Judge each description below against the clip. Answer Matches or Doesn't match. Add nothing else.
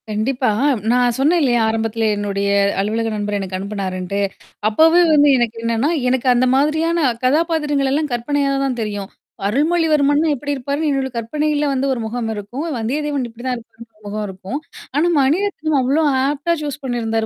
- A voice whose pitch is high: Matches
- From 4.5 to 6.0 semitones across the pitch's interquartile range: Matches